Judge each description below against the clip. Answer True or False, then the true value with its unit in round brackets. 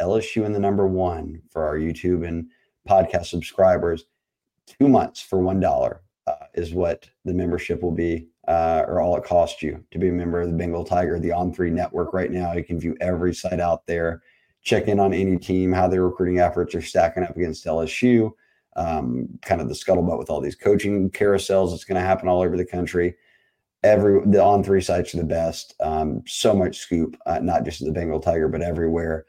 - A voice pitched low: True (90 Hz)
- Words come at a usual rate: False (210 wpm)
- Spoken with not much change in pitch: True (2.0 semitones)